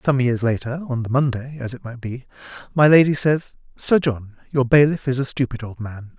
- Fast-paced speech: Yes, fast, 215 wpm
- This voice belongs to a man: Yes, male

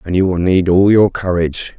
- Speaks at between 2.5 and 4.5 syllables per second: No, 5.4 syllables/s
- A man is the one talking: Yes, male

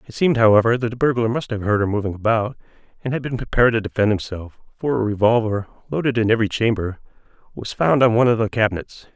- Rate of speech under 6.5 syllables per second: No, 6.9 syllables/s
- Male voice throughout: Yes, male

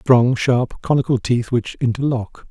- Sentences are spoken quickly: No, average, 145 wpm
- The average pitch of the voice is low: Yes, low, 125 Hz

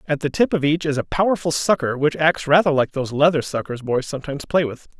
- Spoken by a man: Yes, male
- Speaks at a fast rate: Yes, fast, 240 wpm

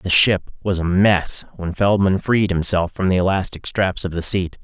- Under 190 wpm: No, fast, 205 wpm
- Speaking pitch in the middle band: No, very low, 95 Hz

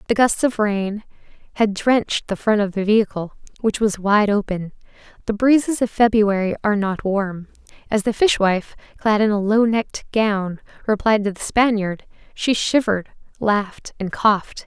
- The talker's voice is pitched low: No, high, 210 Hz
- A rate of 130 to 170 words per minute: Yes, average, 165 wpm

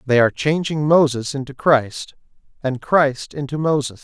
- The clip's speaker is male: Yes, male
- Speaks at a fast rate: No, average, 150 wpm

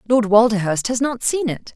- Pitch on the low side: No, high, 230 Hz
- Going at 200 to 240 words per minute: Yes, fast, 205 wpm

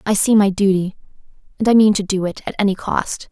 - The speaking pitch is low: No, high, 200 Hz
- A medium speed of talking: No, fast, 235 wpm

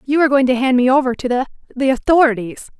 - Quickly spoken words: Yes, fast, 215 wpm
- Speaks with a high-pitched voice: Yes, very high, 255 Hz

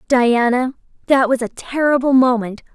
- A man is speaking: No, female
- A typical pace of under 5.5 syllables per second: Yes, 4.7 syllables/s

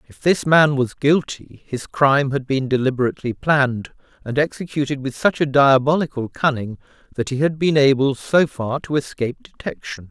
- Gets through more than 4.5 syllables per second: Yes, 5.2 syllables/s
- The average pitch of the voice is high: No, low, 135 Hz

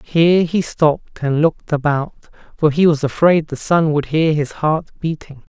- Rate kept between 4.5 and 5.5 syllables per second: Yes, 4.8 syllables/s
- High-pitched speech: No, medium, 155 Hz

